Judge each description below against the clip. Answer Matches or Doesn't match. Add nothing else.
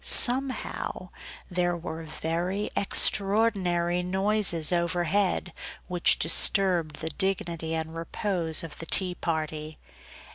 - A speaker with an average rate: Doesn't match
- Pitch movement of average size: Matches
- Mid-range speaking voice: Matches